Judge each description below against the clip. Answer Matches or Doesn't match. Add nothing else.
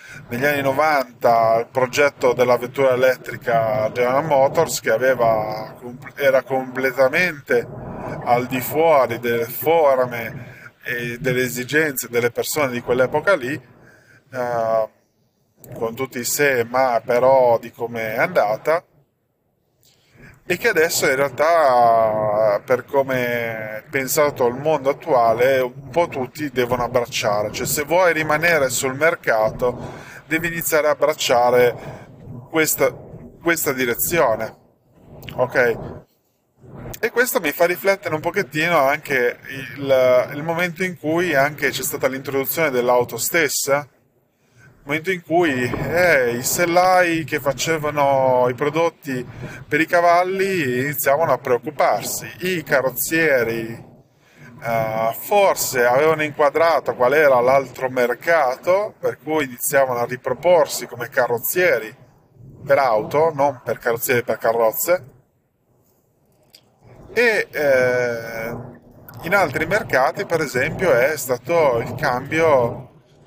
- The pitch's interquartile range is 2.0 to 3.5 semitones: Doesn't match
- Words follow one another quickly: Doesn't match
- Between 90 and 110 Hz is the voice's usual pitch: Doesn't match